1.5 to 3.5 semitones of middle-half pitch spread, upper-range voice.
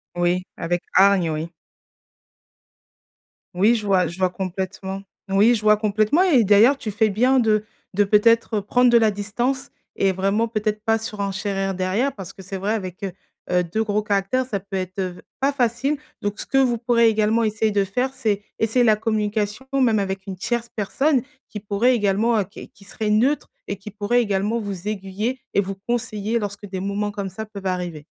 Yes: average, 2.9 semitones; high, 210 Hz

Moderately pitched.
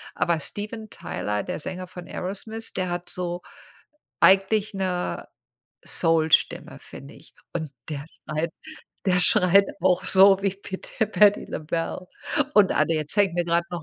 Yes: medium, 180 Hz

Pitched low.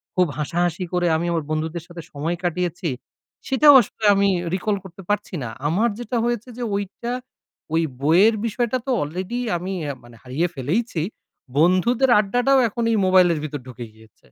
No: medium, 180 Hz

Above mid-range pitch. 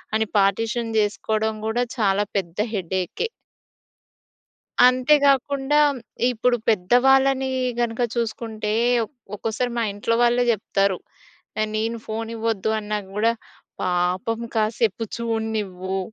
Yes: high, 220 Hz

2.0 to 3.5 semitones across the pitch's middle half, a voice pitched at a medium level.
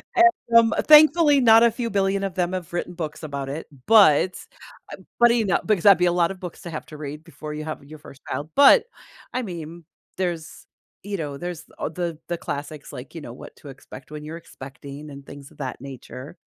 No: average, 4.9 semitones; medium, 170 Hz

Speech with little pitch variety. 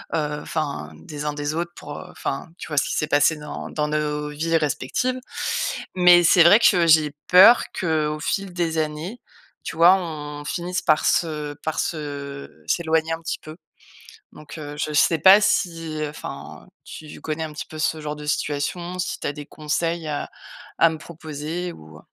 Yes: narrow, 2.3 semitones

